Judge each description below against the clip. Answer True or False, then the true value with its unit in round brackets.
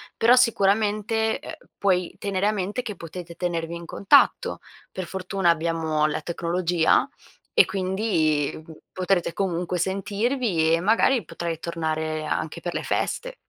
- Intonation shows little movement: False (3.9 semitones)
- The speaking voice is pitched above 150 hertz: True (185 Hz)